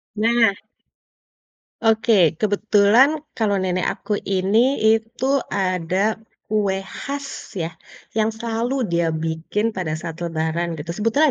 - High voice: Yes, high, 205 Hz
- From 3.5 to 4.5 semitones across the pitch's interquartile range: Yes, average, 4.1 semitones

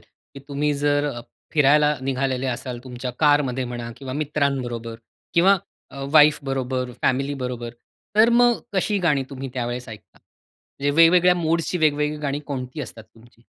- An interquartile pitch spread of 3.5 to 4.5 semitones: No, average, 3.0 semitones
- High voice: No, medium, 140 Hz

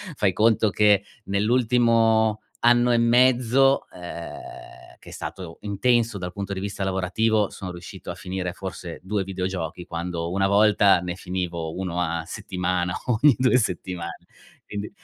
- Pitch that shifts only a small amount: No, average, 3.8 semitones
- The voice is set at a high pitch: No, low, 100 Hz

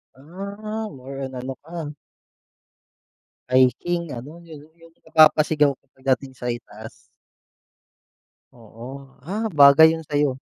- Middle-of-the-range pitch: Yes, medium, 145 Hz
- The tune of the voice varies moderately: Yes, average, 4.2 semitones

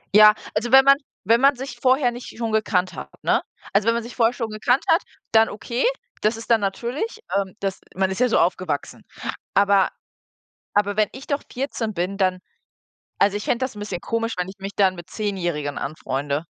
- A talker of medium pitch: No, high, 215 Hz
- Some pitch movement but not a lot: Yes, average, 4.0 semitones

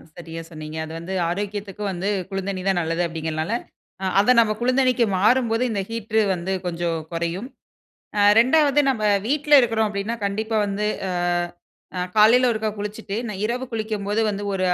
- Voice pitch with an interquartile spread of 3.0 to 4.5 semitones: Yes, average, 3.8 semitones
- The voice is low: No, high, 205 Hz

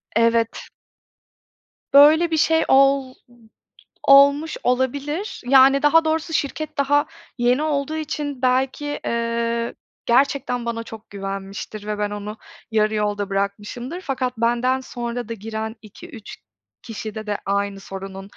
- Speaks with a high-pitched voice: Yes, high, 245 Hz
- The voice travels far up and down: No, average, 4.7 semitones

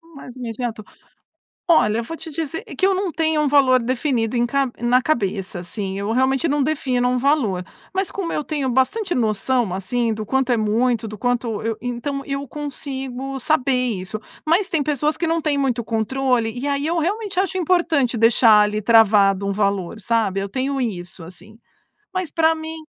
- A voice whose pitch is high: Yes, very high, 255 Hz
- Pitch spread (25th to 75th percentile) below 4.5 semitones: No, average, 5.3 semitones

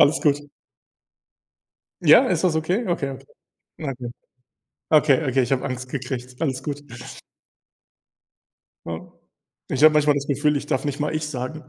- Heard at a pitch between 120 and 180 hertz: Yes, medium, 140 Hz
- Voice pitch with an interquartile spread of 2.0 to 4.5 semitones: Yes, average, 2.7 semitones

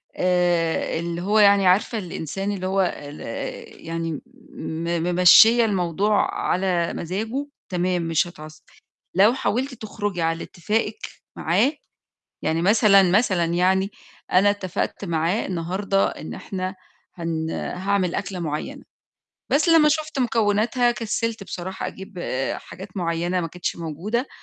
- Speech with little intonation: No, average, 3.5 semitones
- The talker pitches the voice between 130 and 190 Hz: Yes, medium, 185 Hz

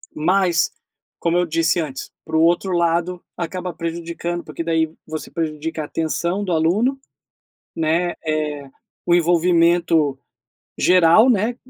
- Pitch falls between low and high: Yes, medium, 170 Hz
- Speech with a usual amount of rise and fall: No, narrow, 1.7 semitones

